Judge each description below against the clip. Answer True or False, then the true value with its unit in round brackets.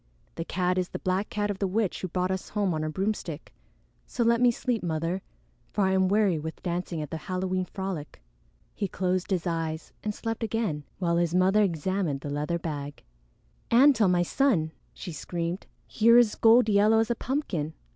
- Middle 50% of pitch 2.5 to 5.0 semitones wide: True (4.1 semitones)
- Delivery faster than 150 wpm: True (190 wpm)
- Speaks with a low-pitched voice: False (185 Hz)